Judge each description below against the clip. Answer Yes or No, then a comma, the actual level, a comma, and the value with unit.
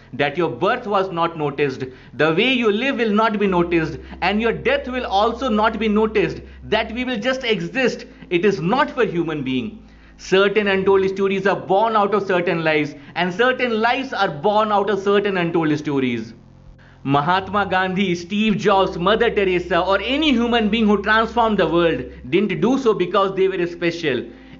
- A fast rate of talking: No, average, 180 wpm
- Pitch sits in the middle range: No, high, 195 Hz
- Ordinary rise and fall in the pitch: Yes, average, 4.3 semitones